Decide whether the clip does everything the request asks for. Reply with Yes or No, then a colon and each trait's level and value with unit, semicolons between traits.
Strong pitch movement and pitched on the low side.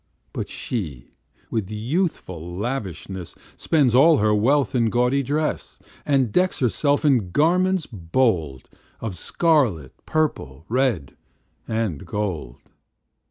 Yes: wide, 7.9 semitones; low, 115 Hz